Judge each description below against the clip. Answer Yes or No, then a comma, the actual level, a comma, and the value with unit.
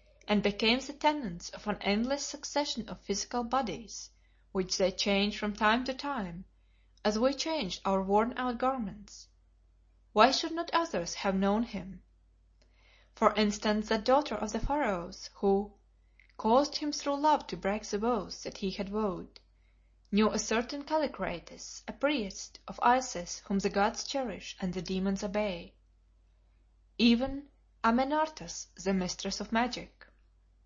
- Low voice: No, high, 210 Hz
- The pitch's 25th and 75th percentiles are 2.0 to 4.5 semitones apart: No, average, 5.2 semitones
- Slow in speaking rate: No, average, 145 wpm